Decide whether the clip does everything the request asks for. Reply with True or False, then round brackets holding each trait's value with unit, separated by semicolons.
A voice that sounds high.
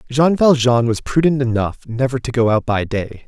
False (125 Hz)